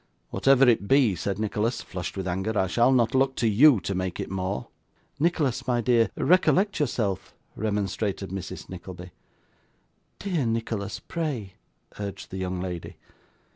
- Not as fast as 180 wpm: Yes, average, 145 wpm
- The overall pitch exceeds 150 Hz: No, low, 110 Hz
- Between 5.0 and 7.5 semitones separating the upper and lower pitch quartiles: Yes, wide, 5.4 semitones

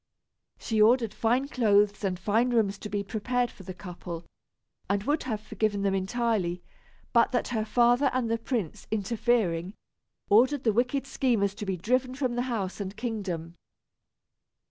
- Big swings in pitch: No, average, 3.6 semitones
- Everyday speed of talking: Yes, average, 160 wpm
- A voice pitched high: Yes, high, 220 Hz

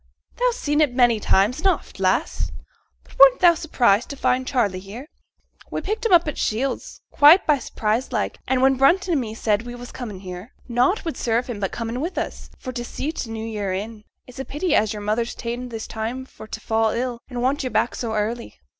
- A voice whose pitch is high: Yes, high, 245 Hz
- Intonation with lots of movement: No, average, 4.0 semitones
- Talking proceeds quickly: Yes, fast, 230 wpm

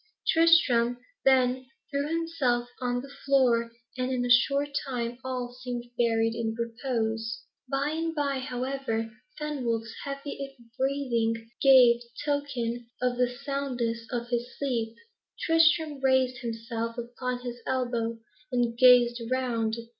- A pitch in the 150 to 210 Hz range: No, very high, 250 Hz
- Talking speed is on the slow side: Yes, slow, 125 wpm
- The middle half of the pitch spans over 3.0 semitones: No, narrow, 2.6 semitones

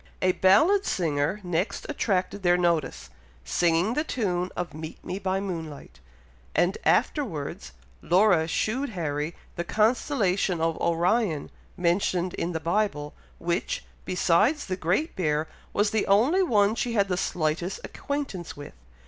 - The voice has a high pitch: No, medium, 180 Hz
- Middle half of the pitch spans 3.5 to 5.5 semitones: Yes, average, 4.2 semitones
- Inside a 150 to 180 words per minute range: No, slow, 135 wpm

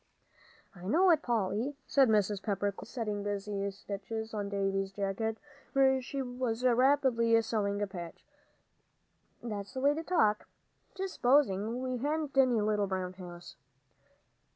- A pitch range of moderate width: Yes, average, 4.5 semitones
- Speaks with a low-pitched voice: No, high, 220 Hz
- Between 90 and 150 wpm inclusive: Yes, average, 140 wpm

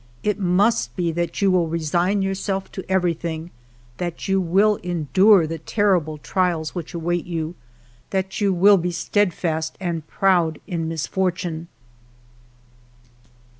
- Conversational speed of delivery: No, slow, 130 wpm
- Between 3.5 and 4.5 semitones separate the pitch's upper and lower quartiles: No, average, 2.7 semitones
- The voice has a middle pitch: Yes, medium, 175 Hz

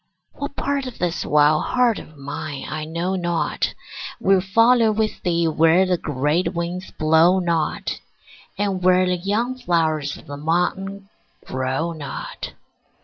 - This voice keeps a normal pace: Yes, average, 145 wpm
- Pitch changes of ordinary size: Yes, average, 3.7 semitones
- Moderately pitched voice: Yes, medium, 175 Hz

